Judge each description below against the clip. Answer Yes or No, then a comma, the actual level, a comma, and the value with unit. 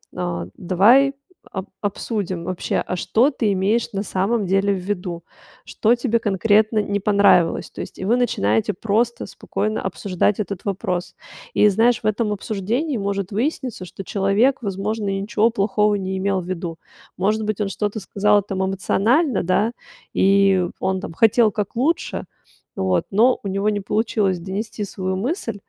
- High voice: Yes, high, 200 Hz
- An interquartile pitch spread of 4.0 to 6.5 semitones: No, narrow, 2.6 semitones